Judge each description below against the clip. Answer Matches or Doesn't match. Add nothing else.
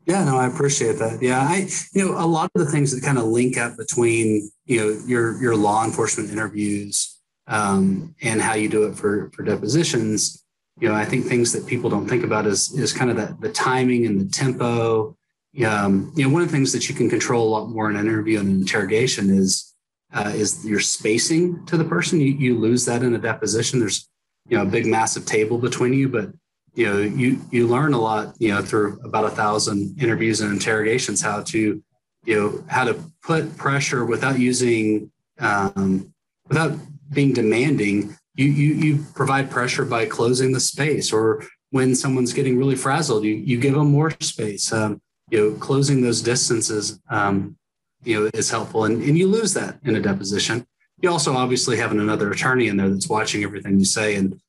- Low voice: Matches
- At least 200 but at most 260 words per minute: Matches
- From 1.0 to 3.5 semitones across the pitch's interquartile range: Doesn't match